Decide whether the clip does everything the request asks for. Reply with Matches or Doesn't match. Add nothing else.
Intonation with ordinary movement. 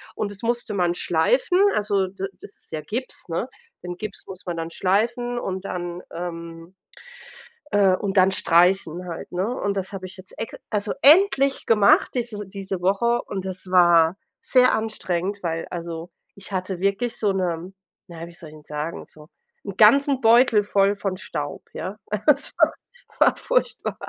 Matches